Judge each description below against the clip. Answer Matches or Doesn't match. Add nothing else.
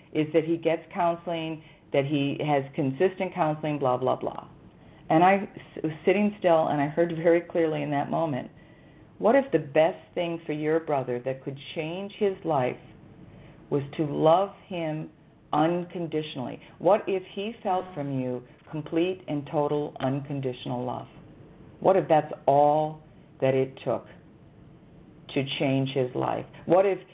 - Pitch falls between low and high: Matches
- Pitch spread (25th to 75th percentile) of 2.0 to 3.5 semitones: Matches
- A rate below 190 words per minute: Matches